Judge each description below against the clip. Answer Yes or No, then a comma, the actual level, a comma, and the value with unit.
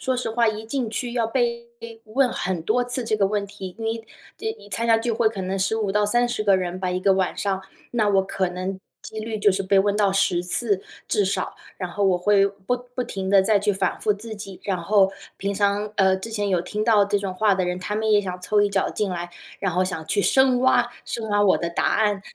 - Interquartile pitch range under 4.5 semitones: Yes, narrow, 2.6 semitones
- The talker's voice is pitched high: Yes, high, 205 Hz